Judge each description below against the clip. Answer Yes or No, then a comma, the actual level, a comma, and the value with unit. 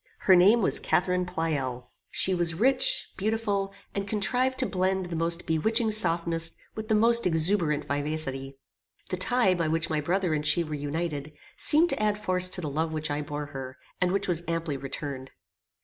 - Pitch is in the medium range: Yes, medium, 170 Hz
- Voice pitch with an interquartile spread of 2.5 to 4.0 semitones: No, average, 4.7 semitones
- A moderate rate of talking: Yes, average, 180 wpm